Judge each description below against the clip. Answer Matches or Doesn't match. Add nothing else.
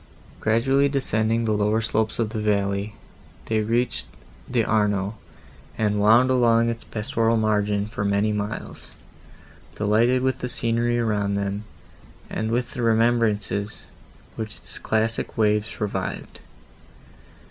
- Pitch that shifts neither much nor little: Doesn't match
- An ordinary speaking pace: Doesn't match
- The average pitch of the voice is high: Doesn't match